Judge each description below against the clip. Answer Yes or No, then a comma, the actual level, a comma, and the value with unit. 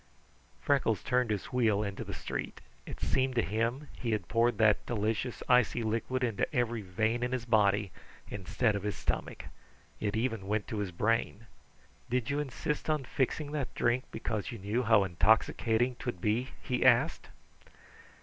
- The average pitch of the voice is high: No, low, 115 Hz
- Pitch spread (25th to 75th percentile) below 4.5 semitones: Yes, average, 3.0 semitones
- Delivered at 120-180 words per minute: Yes, average, 165 wpm